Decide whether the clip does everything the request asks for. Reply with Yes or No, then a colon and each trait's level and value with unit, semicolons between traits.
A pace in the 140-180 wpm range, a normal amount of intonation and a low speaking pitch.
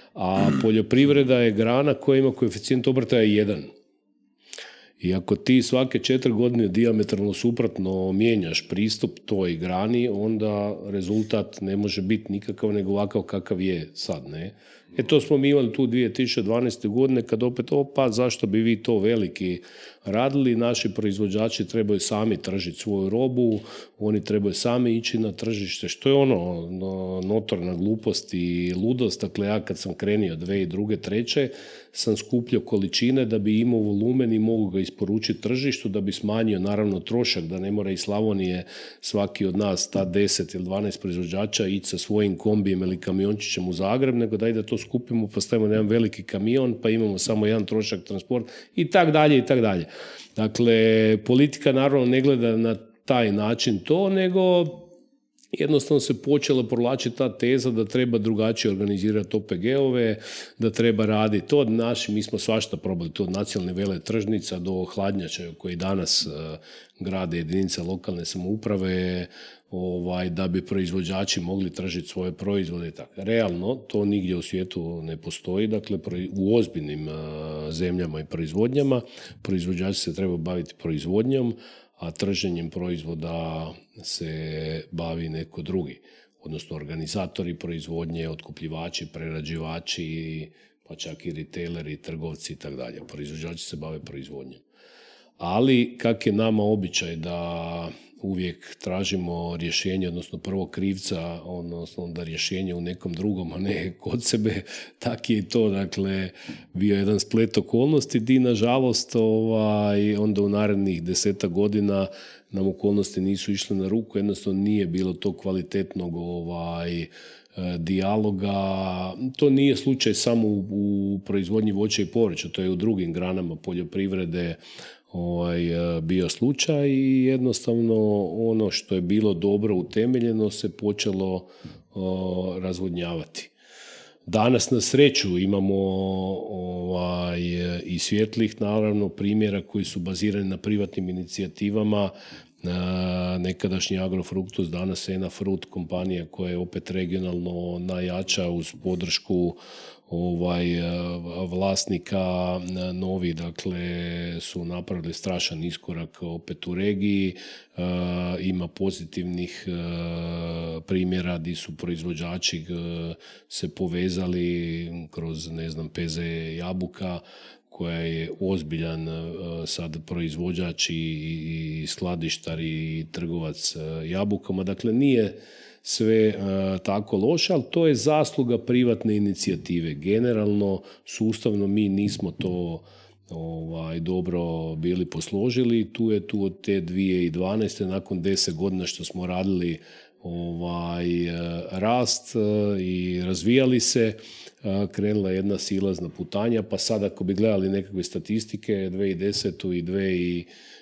No: average, 130 wpm; average, 3.8 semitones; very low, 95 Hz